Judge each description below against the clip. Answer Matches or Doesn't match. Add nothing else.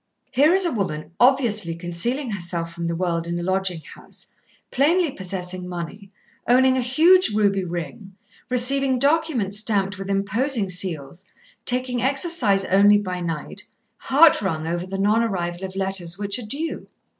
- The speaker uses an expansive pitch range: Matches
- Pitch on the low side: Doesn't match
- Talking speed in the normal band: Matches